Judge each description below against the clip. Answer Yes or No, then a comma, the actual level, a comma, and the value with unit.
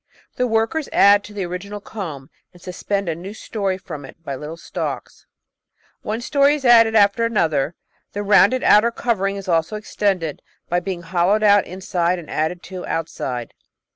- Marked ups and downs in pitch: No, average, 3.8 semitones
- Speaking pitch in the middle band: No, high, 195 Hz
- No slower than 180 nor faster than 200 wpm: No, average, 170 wpm